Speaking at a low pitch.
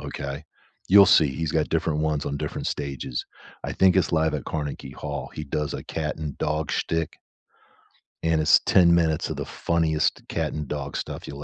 Yes: very low, 75 Hz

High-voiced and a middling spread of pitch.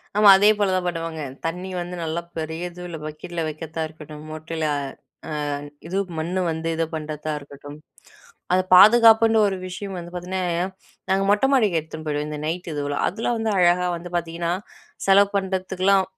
No: medium, 175 Hz; average, 3.2 semitones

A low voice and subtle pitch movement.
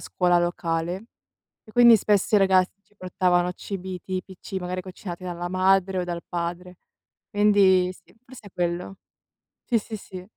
No: medium, 185 Hz; narrow, 1.7 semitones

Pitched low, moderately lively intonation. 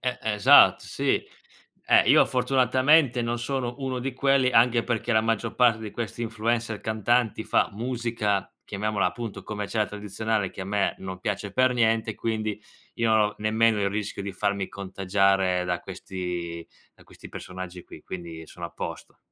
Yes: low, 110 Hz; average, 3.3 semitones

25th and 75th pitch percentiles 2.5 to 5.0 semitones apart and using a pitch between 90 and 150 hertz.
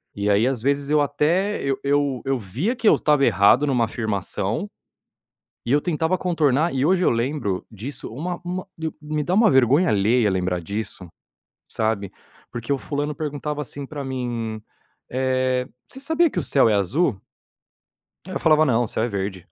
No: wide, 5.4 semitones; low, 135 Hz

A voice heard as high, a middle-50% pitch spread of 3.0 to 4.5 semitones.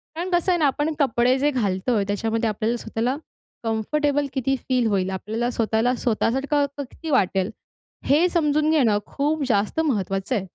No: very high, 250 Hz; average, 5.0 semitones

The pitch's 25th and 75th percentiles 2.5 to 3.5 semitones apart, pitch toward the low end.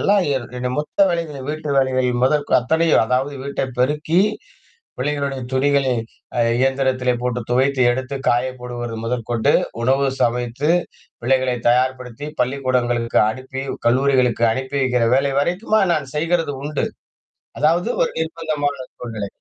Yes: average, 2.8 semitones; low, 130 Hz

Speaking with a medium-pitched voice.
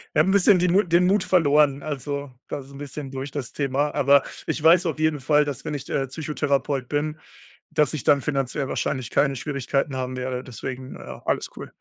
Yes: medium, 145 Hz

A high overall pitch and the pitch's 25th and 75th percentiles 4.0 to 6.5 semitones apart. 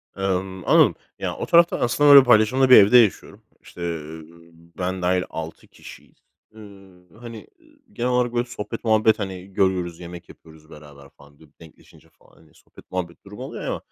No: very low, 95 Hz; average, 5.1 semitones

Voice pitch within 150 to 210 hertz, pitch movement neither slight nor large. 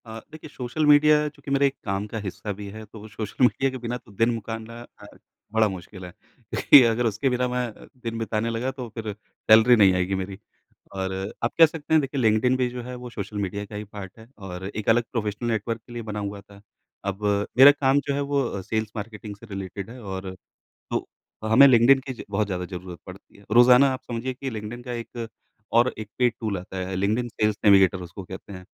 No: low, 110 Hz; average, 3.7 semitones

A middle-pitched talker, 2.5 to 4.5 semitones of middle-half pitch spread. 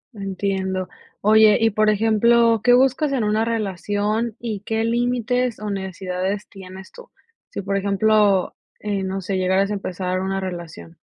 No: high, 205 Hz; average, 2.8 semitones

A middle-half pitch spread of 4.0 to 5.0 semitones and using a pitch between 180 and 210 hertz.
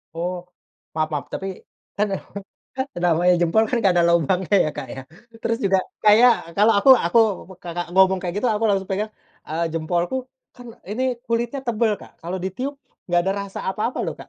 Yes: average, 4.3 semitones; high, 190 Hz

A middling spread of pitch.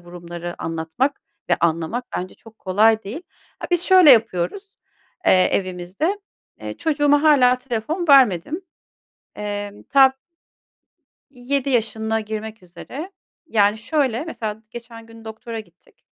No: wide, 5.8 semitones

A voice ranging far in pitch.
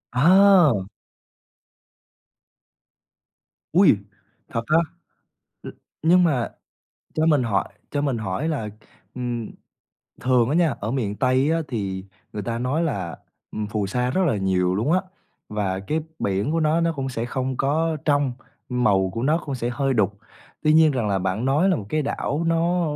Yes: wide, 6.6 semitones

